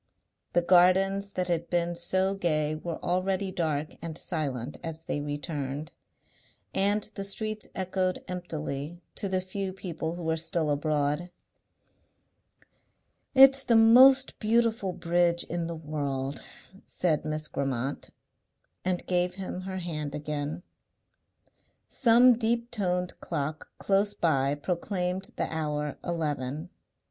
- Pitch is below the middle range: No, medium, 175 Hz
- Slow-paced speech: Yes, slow, 120 wpm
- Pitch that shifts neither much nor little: Yes, average, 4.0 semitones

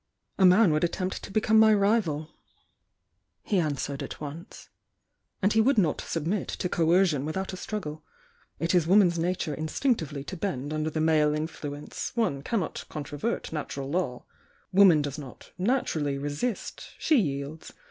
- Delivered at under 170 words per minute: Yes, average, 155 wpm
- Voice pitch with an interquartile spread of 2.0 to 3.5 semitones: No, average, 4.9 semitones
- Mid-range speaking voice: Yes, medium, 165 Hz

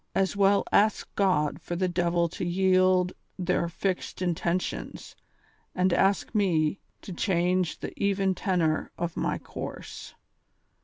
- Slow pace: Yes, slow, 125 wpm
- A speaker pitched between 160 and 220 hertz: Yes, medium, 185 Hz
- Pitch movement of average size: No, narrow, 1.9 semitones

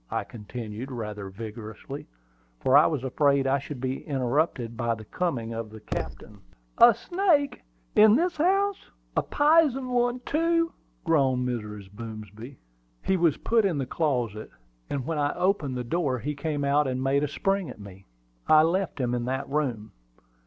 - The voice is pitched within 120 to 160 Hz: Yes, medium, 140 Hz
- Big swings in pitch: Yes, wide, 7.5 semitones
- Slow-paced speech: No, average, 165 wpm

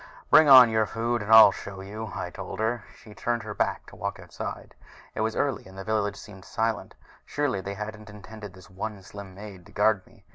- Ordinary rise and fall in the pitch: No, narrow, 2.1 semitones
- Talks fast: Yes, fast, 220 wpm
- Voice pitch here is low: Yes, low, 105 Hz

